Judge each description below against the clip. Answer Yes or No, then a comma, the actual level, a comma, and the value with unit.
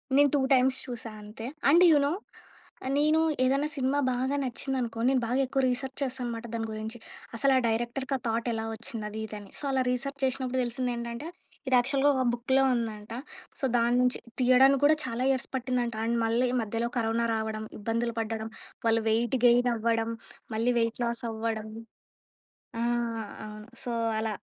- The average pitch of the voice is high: Yes, high, 240 Hz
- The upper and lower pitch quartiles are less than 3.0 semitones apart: Yes, narrow, 2.6 semitones